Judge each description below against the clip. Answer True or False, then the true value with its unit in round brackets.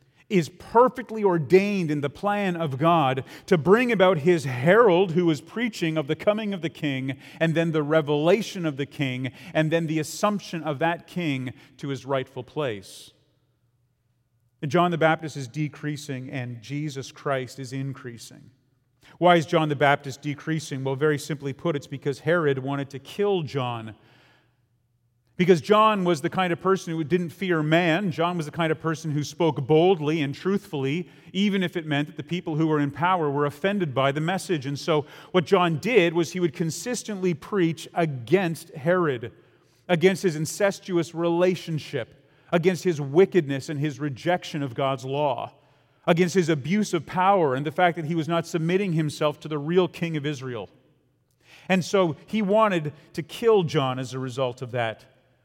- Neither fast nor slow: True (175 wpm)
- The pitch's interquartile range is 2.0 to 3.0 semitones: False (4.2 semitones)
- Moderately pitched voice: True (155 Hz)